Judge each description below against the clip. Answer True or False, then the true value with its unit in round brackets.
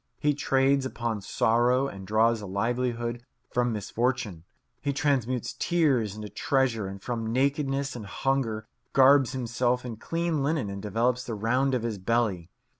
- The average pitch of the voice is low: True (120 Hz)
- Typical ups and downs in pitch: True (3.6 semitones)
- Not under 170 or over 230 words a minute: False (150 wpm)